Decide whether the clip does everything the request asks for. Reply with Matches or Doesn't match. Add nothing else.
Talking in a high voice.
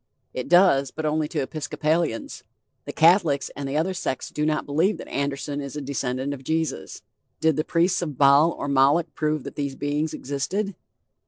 Doesn't match